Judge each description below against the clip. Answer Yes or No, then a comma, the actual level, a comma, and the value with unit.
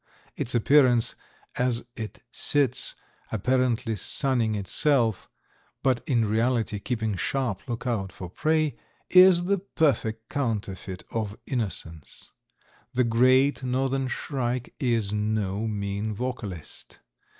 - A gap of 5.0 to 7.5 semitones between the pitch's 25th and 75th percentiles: No, average, 3.6 semitones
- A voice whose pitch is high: No, low, 120 Hz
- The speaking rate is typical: No, slow, 105 wpm